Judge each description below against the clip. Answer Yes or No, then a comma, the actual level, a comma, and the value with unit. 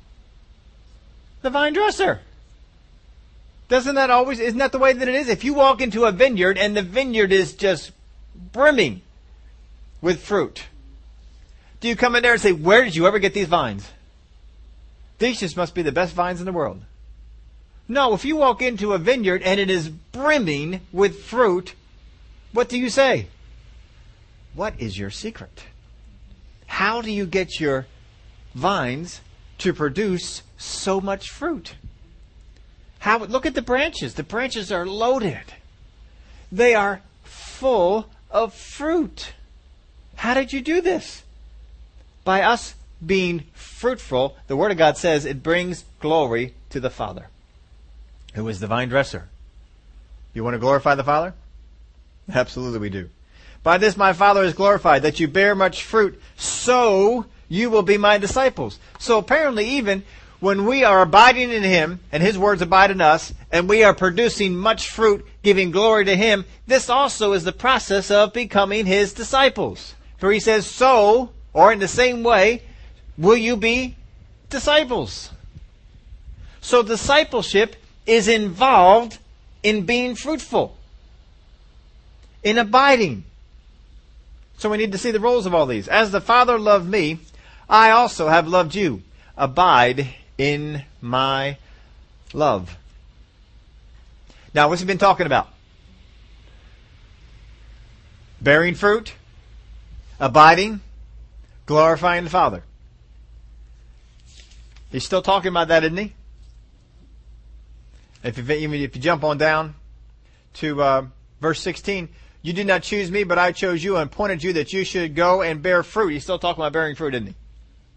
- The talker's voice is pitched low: No, medium, 180 Hz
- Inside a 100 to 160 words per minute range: Yes, average, 145 wpm